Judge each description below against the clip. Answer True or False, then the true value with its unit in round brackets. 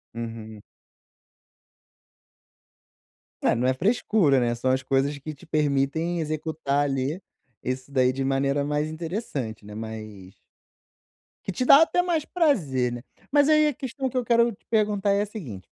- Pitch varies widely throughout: True (8.5 semitones)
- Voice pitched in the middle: True (145 Hz)